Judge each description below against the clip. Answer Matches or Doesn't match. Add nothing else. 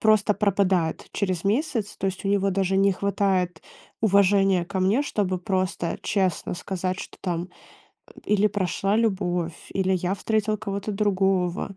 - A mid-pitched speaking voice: Doesn't match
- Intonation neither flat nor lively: Doesn't match